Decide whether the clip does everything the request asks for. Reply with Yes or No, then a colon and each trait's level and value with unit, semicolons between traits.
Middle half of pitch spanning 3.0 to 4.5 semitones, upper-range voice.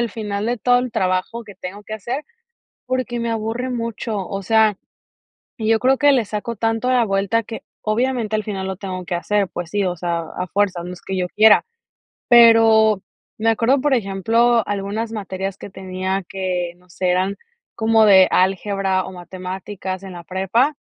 Yes: average, 3.3 semitones; high, 205 Hz